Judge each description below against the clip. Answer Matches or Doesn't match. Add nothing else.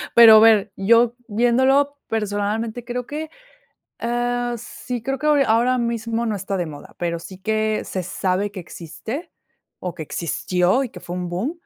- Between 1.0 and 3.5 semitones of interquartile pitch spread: Doesn't match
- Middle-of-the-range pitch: Doesn't match